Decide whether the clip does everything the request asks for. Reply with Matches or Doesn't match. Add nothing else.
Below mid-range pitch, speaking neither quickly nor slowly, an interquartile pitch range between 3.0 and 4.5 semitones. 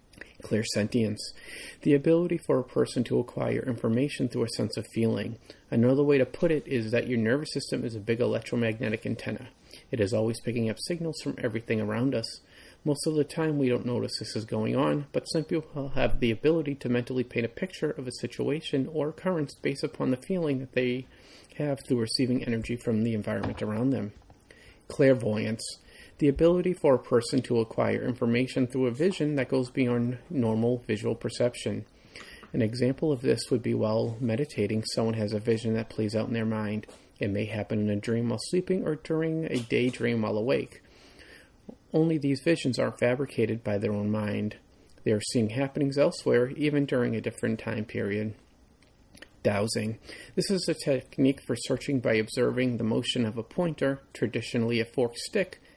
Matches